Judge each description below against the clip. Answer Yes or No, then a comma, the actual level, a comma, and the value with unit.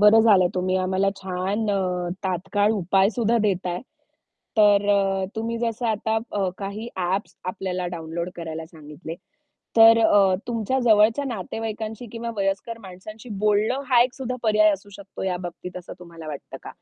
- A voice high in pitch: Yes, high, 200 Hz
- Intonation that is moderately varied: Yes, average, 3.3 semitones